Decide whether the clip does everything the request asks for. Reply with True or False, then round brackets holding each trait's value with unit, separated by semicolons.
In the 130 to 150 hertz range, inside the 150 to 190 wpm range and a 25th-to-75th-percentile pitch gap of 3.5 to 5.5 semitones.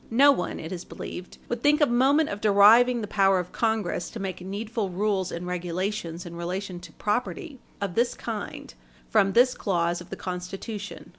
False (200 Hz; 180 wpm; 4.3 semitones)